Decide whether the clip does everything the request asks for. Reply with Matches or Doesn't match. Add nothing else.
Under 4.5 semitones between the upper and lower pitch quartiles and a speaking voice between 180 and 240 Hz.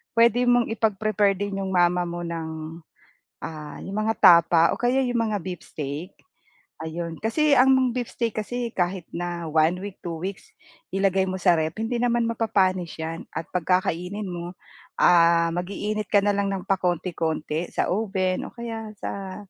Matches